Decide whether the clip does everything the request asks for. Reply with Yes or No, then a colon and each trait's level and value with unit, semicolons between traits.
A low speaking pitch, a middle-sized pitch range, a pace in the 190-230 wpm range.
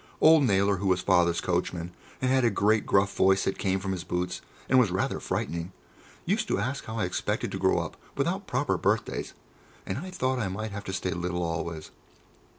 Yes: very low, 95 Hz; average, 3.5 semitones; fast, 205 wpm